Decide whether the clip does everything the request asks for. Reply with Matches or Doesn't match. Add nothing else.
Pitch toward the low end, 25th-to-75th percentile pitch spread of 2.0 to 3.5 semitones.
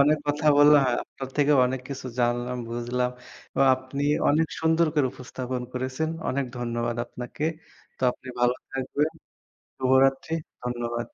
Matches